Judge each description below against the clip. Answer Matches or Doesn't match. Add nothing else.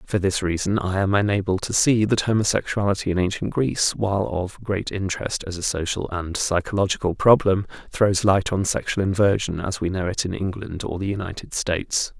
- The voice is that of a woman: Doesn't match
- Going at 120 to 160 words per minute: Doesn't match